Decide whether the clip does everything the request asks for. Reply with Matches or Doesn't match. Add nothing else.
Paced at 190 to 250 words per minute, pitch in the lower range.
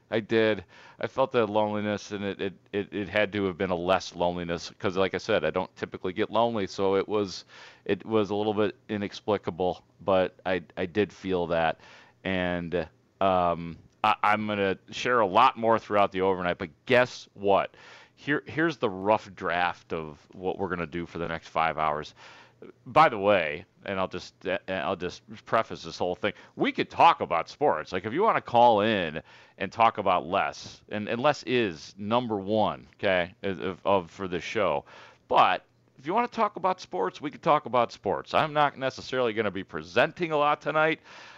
Matches